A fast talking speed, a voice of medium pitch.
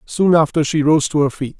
Yes: fast, 265 wpm; medium, 150 Hz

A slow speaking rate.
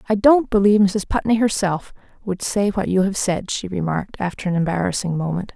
No: average, 195 wpm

